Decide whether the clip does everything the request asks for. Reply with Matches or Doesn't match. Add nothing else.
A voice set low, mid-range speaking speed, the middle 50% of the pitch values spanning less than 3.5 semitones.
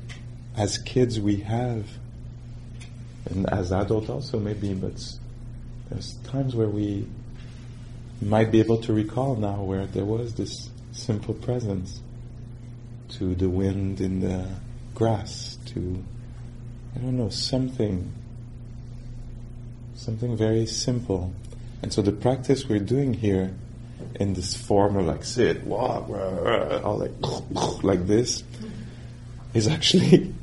Doesn't match